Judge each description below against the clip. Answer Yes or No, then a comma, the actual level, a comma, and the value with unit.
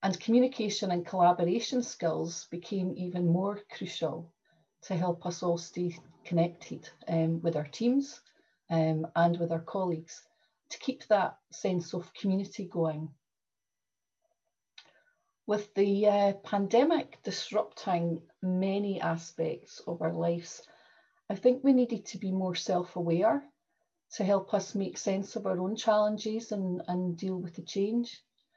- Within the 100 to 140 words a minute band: Yes, slow, 135 wpm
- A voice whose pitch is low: No, high, 190 Hz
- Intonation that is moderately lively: Yes, average, 4.4 semitones